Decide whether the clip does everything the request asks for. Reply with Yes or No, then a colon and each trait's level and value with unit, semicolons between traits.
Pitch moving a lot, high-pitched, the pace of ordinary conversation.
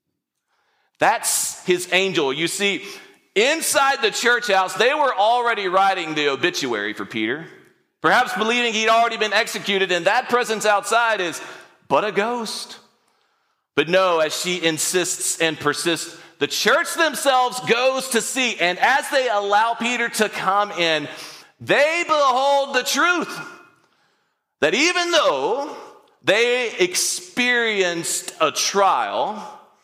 No: wide, 7.3 semitones; high, 225 Hz; slow, 125 wpm